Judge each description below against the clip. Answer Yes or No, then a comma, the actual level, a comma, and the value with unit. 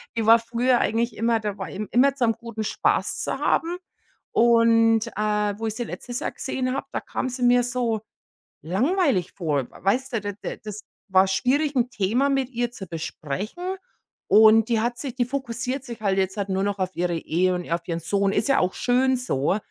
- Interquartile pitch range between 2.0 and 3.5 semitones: No, average, 4.2 semitones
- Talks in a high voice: Yes, high, 225 Hz